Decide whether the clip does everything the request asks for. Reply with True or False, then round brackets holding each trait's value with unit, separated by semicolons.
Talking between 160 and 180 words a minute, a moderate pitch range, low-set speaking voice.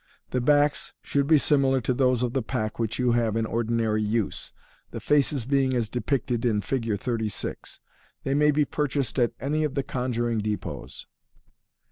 True (170 wpm; 3.4 semitones; 125 Hz)